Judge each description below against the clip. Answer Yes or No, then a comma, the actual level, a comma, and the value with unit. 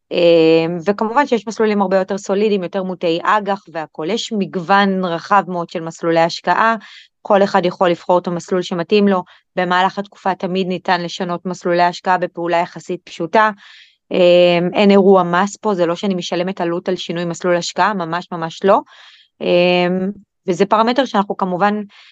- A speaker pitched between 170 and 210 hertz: Yes, medium, 185 Hz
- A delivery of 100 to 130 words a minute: No, fast, 150 wpm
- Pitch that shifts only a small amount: Yes, narrow, 2.3 semitones